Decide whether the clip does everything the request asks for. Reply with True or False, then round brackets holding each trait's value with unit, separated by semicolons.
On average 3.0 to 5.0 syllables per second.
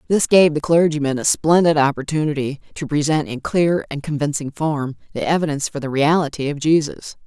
False (5.6 syllables/s)